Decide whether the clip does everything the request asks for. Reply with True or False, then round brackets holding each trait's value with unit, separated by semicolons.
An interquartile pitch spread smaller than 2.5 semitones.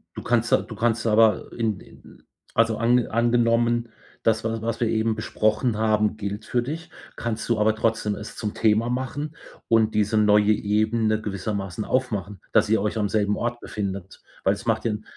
True (1.7 semitones)